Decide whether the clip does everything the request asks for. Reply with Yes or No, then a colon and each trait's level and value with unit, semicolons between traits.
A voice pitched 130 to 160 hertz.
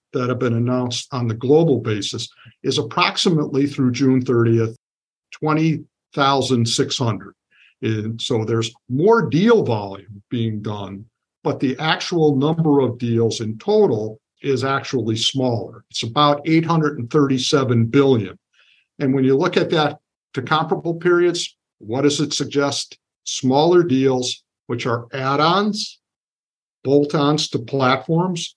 Yes: low, 135 Hz